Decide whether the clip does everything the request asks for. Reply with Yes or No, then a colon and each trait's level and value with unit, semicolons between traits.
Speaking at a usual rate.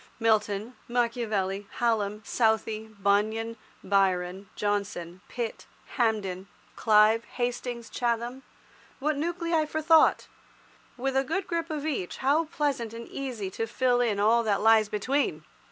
No: slow, 120 wpm